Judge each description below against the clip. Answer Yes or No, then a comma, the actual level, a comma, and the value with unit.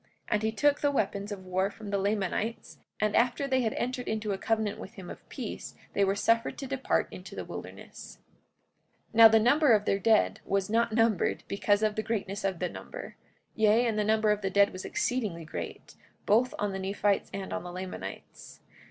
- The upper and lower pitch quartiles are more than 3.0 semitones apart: No, narrow, 2.6 semitones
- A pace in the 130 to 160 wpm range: No, fast, 205 wpm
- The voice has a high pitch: Yes, high, 210 Hz